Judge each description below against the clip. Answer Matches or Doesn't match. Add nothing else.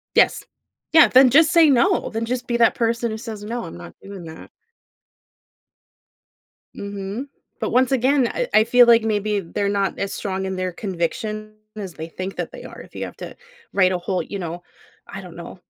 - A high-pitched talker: Matches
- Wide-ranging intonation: Doesn't match